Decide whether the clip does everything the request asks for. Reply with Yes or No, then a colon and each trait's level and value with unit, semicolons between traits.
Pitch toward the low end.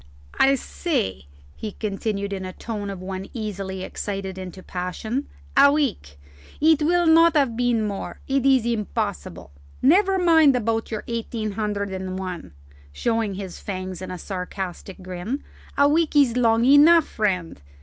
No: high, 215 Hz